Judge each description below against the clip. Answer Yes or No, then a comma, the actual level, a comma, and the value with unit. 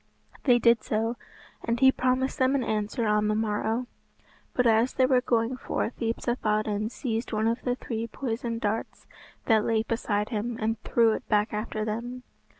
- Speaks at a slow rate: No, average, 170 wpm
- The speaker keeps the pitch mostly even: Yes, narrow, 2.3 semitones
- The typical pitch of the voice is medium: No, high, 230 Hz